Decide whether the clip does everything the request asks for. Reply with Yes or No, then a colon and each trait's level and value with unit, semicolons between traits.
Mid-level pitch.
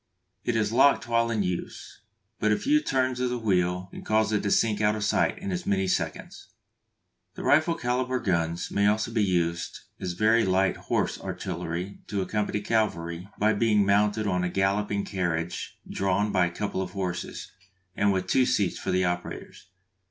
No: low, 100 Hz